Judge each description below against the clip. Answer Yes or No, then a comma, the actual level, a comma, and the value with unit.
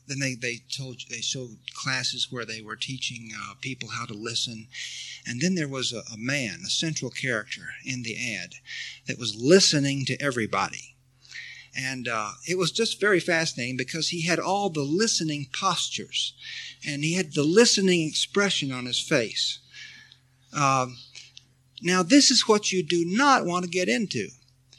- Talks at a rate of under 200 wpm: Yes, average, 165 wpm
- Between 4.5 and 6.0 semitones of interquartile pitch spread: Yes, wide, 5.6 semitones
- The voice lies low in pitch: Yes, low, 130 Hz